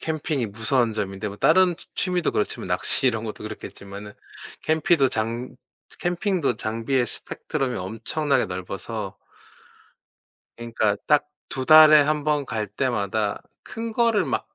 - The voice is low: Yes, low, 125 Hz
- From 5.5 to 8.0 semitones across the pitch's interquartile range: Yes, wide, 6.2 semitones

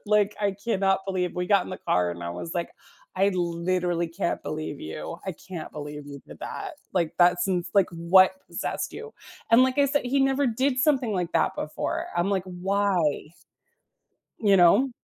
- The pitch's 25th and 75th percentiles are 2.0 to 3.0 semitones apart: No, average, 3.8 semitones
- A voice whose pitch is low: No, medium, 185 Hz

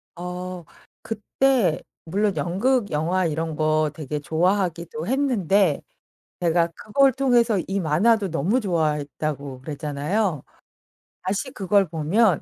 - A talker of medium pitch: Yes, medium, 180 Hz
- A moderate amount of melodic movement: Yes, average, 5.0 semitones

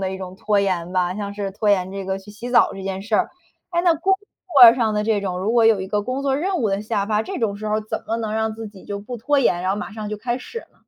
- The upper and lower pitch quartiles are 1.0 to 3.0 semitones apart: Yes, average, 2.7 semitones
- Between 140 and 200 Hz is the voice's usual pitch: No, high, 210 Hz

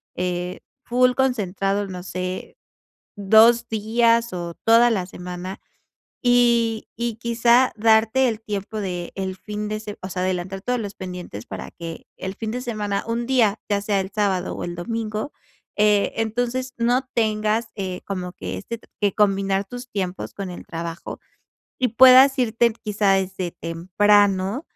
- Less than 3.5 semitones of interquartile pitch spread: No, average, 3.8 semitones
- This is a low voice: No, high, 210 Hz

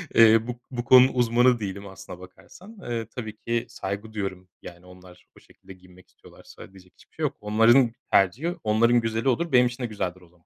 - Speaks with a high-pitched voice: No, low, 110 Hz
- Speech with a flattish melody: No, average, 4.5 semitones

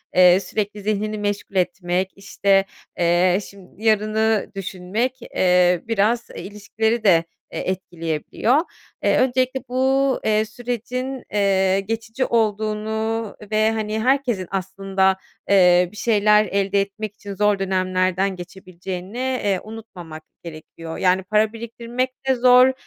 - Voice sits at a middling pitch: No, high, 205 Hz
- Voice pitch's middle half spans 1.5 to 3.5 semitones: Yes, average, 3.1 semitones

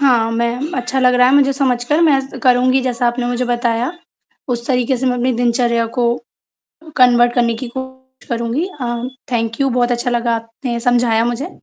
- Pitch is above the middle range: Yes, high, 245 Hz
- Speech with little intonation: Yes, narrow, 1.6 semitones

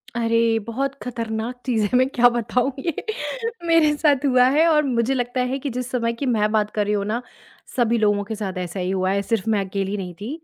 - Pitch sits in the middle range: No, high, 230 Hz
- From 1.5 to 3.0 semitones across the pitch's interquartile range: No, average, 3.6 semitones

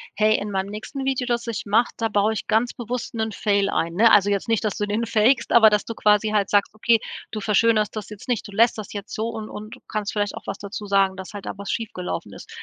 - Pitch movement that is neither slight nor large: No, narrow, 2.0 semitones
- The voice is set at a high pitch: Yes, high, 215 Hz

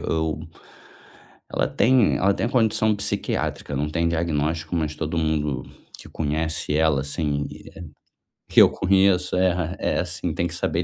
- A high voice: No, very low, 80 Hz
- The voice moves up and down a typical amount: Yes, average, 3.1 semitones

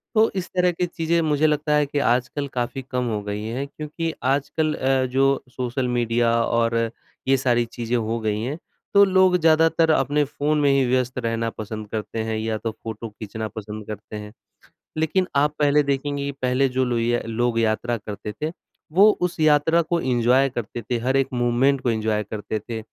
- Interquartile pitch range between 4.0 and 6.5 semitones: Yes, average, 4.5 semitones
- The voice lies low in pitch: Yes, low, 125 Hz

